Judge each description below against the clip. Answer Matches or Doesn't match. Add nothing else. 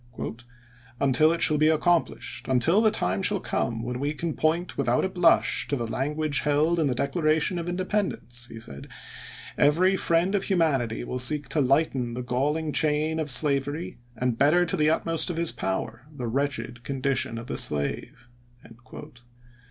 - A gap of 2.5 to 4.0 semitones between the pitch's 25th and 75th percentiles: Doesn't match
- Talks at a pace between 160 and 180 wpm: Matches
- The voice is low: Doesn't match